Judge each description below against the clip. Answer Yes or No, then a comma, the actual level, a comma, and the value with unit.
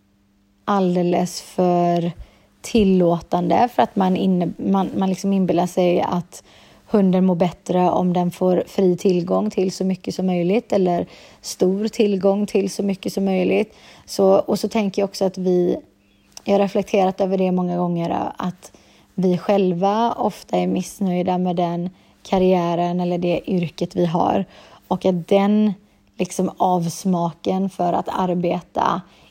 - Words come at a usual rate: Yes, average, 145 wpm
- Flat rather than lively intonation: Yes, narrow, 1.9 semitones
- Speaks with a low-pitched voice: No, medium, 185 Hz